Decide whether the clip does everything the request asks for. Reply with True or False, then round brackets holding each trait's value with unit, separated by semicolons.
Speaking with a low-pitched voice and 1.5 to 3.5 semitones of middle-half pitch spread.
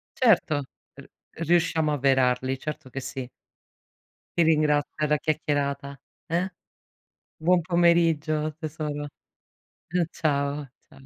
False (150 Hz; 2.6 semitones)